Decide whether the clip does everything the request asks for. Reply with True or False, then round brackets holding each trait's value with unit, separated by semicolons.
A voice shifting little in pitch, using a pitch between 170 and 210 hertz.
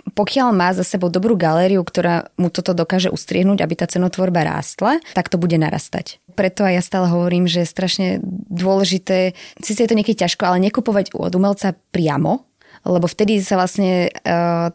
True (2.0 semitones; 185 Hz)